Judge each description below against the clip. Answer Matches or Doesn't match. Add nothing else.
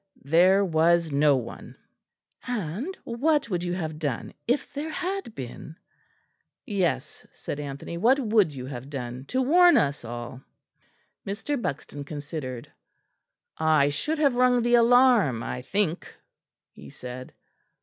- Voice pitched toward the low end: Doesn't match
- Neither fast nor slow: Doesn't match